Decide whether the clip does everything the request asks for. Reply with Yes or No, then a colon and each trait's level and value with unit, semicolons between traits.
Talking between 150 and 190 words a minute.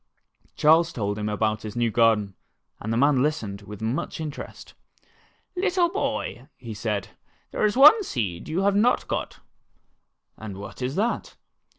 Yes: average, 160 wpm